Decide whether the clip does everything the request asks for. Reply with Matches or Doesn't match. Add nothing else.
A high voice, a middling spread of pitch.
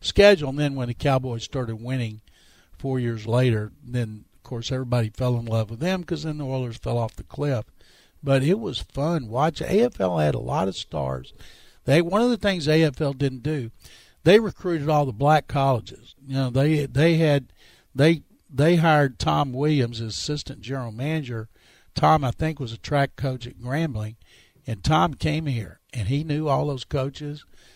Doesn't match